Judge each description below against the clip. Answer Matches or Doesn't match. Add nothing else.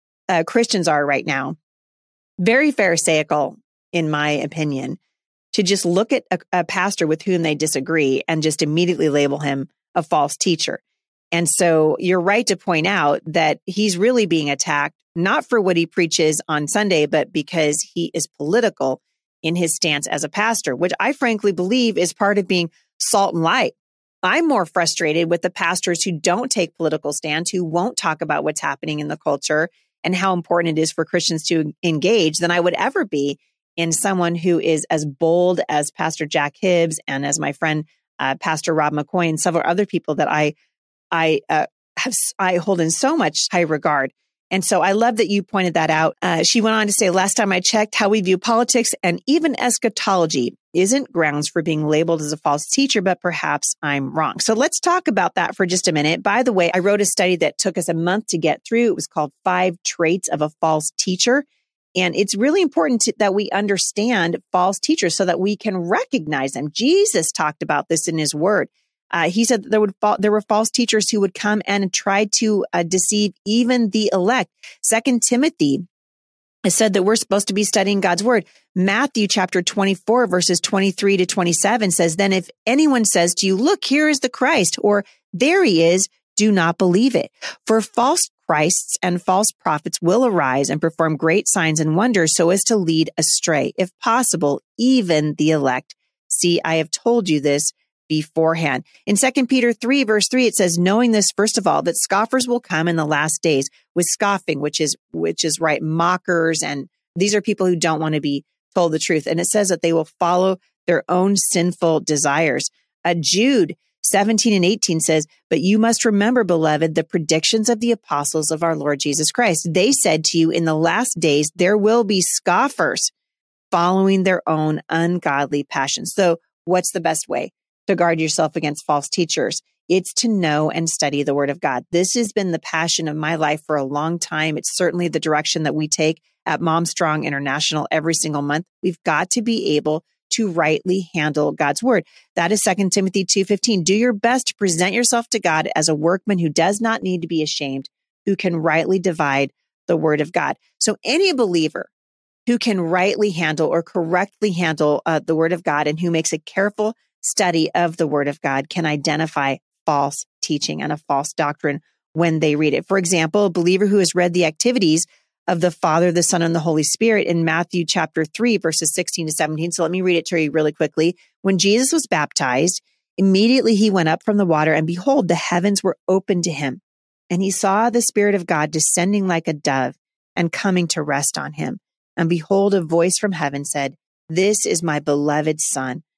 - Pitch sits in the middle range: Matches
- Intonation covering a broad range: Doesn't match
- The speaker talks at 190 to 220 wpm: Matches